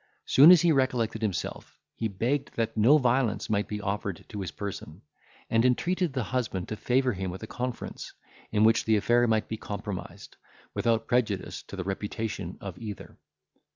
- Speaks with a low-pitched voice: Yes, low, 110 Hz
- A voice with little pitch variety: No, average, 3.5 semitones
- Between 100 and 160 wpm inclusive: No, average, 175 wpm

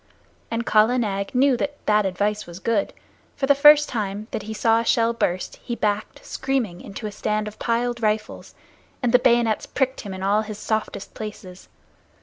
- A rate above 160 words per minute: Yes, average, 180 wpm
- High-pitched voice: Yes, high, 215 Hz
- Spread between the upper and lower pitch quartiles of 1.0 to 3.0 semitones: Yes, average, 2.7 semitones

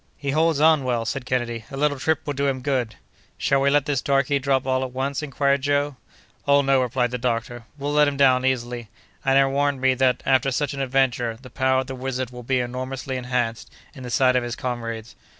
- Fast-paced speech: Yes, fast, 225 wpm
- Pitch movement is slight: Yes, narrow, 1.9 semitones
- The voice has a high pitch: No, low, 130 Hz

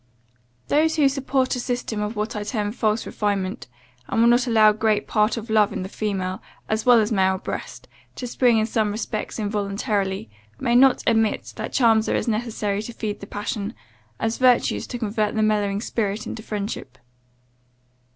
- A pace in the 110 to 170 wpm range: No, average, 180 wpm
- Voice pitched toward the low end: No, high, 215 Hz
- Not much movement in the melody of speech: Yes, narrow, 2.3 semitones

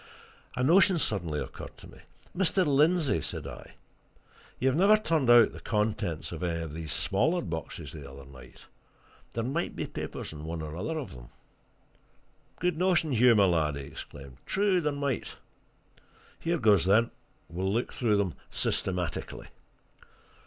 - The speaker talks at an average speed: Yes, average, 155 wpm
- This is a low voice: Yes, low, 110 Hz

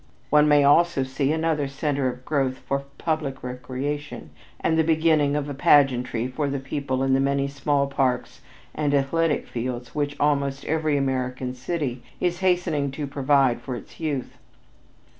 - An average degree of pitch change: No, narrow, 2.2 semitones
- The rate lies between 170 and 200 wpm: No, average, 160 wpm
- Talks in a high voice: No, medium, 140 Hz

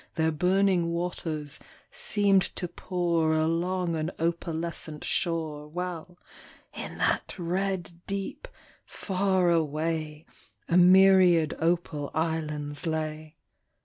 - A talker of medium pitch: Yes, medium, 170 Hz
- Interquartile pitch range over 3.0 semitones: No, narrow, 2.4 semitones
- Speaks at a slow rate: Yes, slow, 95 wpm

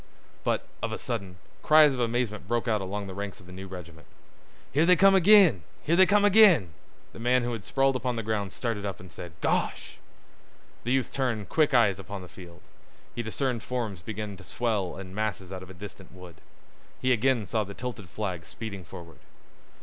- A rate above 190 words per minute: Yes, average, 200 wpm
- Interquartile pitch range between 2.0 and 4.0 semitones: No, average, 5.0 semitones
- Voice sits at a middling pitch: No, low, 110 Hz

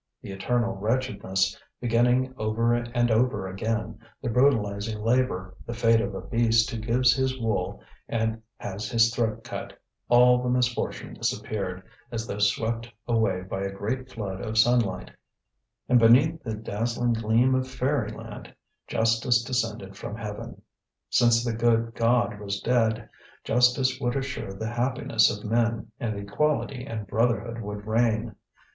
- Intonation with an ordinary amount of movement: No, narrow, 2.2 semitones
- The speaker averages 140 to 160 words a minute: Yes, average, 145 wpm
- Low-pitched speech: Yes, low, 115 Hz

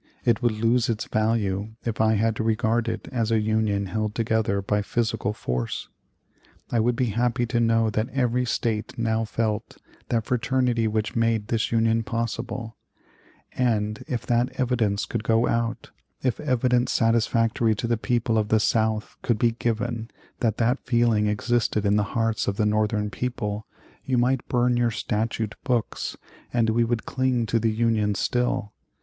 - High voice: No, low, 115 Hz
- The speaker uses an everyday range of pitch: No, narrow, 1.7 semitones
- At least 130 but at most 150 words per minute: No, average, 165 wpm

